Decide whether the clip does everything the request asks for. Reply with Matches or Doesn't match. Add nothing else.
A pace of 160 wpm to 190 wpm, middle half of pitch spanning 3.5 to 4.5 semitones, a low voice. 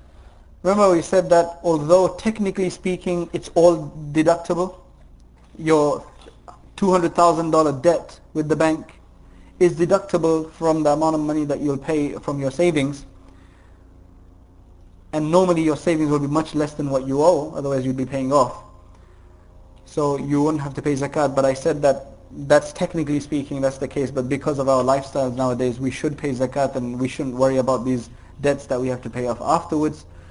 Doesn't match